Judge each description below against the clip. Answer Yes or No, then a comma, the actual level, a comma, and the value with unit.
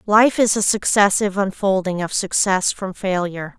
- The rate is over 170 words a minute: No, average, 150 wpm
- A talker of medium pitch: No, high, 195 Hz